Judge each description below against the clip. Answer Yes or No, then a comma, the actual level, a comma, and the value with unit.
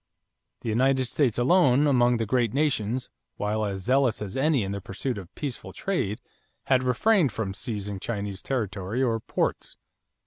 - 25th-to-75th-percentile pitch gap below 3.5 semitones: No, average, 4.4 semitones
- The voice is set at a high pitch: No, low, 120 Hz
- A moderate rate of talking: Yes, average, 160 wpm